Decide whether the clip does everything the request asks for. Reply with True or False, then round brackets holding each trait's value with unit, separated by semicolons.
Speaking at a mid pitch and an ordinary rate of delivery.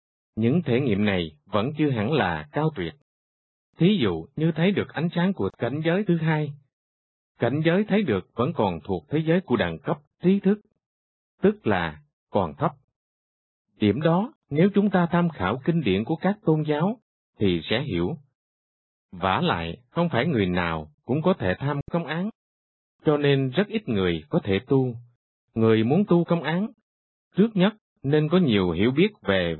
True (145 Hz; 180 wpm)